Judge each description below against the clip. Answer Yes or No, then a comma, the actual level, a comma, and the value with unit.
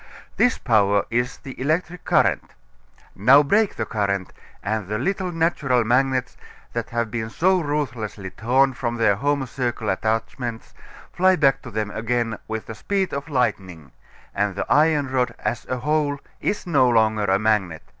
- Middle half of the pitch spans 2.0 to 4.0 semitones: No, average, 4.8 semitones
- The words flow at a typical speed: Yes, average, 160 wpm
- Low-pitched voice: Yes, low, 120 Hz